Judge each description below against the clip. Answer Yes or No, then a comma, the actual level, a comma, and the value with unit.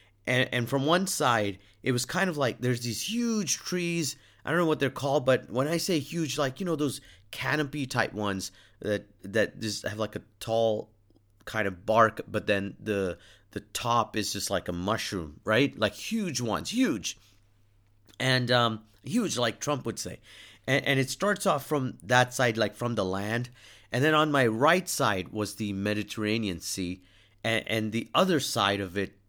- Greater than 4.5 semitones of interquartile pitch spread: Yes, wide, 5.4 semitones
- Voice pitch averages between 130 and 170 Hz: No, low, 115 Hz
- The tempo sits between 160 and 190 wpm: Yes, average, 185 wpm